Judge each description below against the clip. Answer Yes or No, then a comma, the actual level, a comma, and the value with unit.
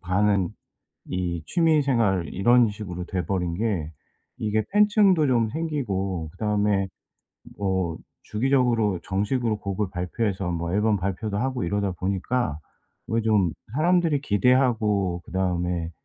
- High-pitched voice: No, low, 105 Hz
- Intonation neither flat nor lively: Yes, average, 4.8 semitones